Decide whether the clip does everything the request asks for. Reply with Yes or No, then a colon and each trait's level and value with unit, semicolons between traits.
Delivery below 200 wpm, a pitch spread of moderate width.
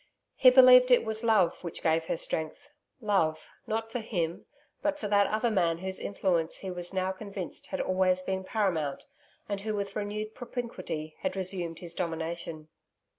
Yes: average, 175 wpm; average, 4.3 semitones